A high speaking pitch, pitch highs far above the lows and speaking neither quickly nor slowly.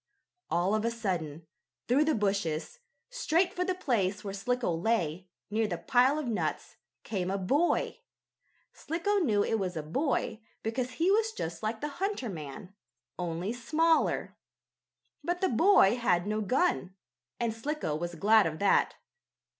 Yes: high, 220 Hz; wide, 8.3 semitones; average, 155 wpm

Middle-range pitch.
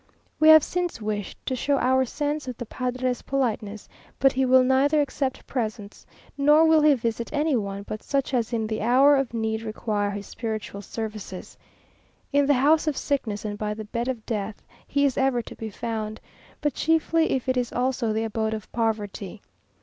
No: high, 245 Hz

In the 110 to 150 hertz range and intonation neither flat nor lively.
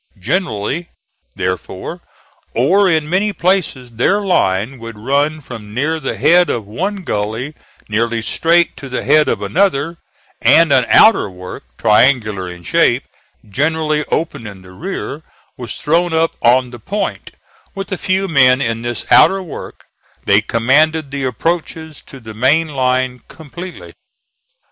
No: medium, 140 Hz; wide, 6.3 semitones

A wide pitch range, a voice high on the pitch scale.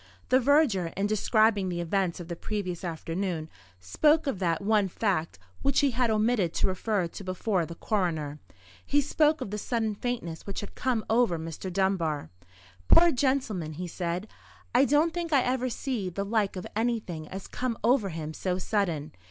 Yes: wide, 6.0 semitones; high, 200 Hz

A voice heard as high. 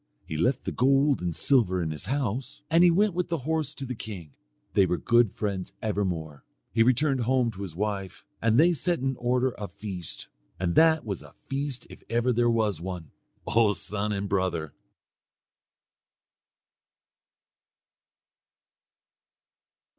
No: low, 115 Hz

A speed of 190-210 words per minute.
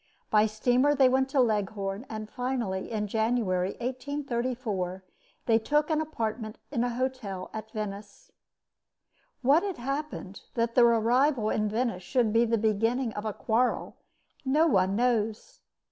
No: average, 145 wpm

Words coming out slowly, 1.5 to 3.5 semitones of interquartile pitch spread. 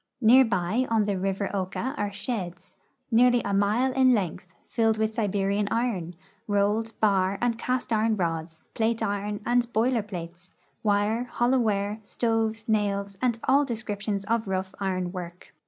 No: average, 155 wpm; average, 2.8 semitones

